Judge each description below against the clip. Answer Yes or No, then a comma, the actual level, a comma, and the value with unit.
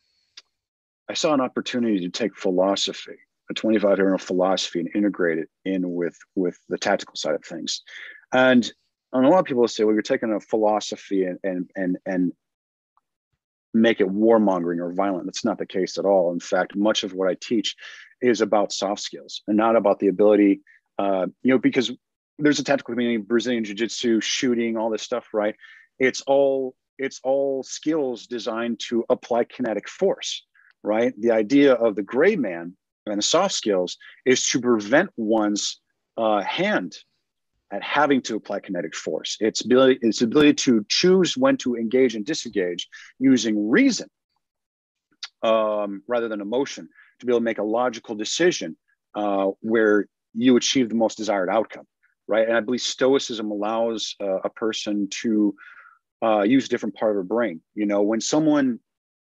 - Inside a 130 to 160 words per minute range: No, average, 170 wpm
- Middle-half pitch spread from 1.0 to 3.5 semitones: No, average, 4.0 semitones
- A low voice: Yes, low, 115 Hz